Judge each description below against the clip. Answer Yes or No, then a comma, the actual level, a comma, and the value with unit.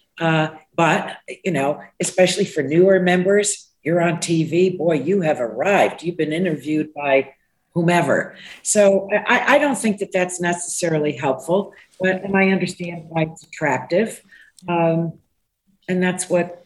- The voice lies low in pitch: No, medium, 175 Hz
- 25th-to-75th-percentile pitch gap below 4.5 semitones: Yes, average, 2.7 semitones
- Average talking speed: Yes, average, 145 wpm